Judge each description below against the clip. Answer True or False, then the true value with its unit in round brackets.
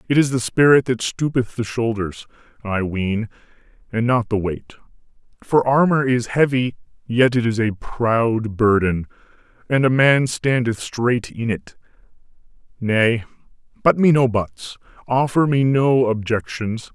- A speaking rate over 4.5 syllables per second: False (4.1 syllables/s)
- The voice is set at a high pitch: False (120 Hz)